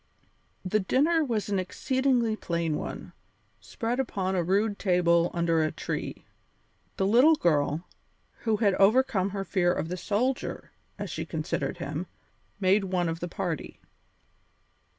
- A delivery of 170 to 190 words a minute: No, average, 140 wpm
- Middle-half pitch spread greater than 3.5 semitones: Yes, average, 4.4 semitones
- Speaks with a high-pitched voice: Yes, high, 195 Hz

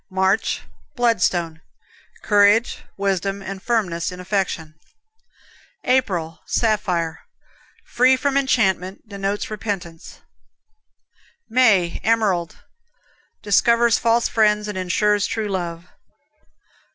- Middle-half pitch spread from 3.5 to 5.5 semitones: Yes, average, 3.8 semitones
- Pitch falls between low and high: No, high, 200 Hz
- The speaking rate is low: Yes, slow, 85 wpm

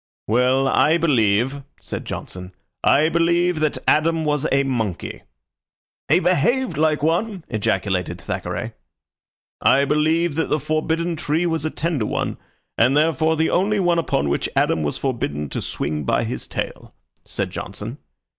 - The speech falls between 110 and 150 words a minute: Yes, average, 145 wpm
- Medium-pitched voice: Yes, medium, 150 Hz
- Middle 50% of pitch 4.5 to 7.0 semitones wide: Yes, wide, 5.4 semitones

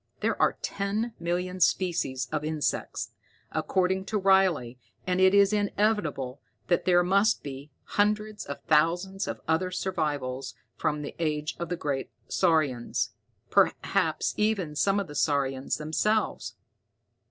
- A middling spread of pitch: Yes, average, 4.8 semitones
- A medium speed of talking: No, slow, 130 wpm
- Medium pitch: Yes, medium, 175 Hz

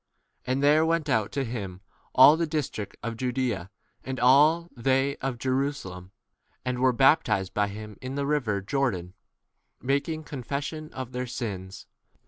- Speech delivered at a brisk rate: No, average, 155 wpm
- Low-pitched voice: Yes, low, 130 Hz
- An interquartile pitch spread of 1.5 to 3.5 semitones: No, average, 4.8 semitones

